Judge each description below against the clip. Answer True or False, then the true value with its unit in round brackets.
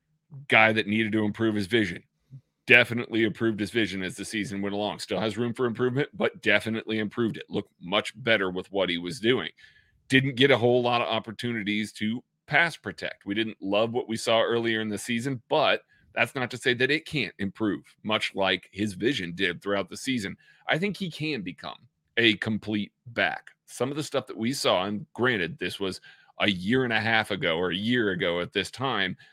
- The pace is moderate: False (210 wpm)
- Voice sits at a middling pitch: False (110 Hz)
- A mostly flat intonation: False (3.2 semitones)